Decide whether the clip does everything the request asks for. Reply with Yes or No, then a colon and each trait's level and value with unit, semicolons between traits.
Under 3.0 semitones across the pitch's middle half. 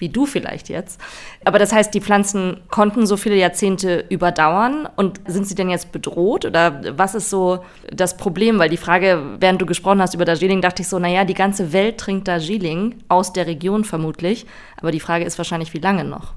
Yes: narrow, 2.6 semitones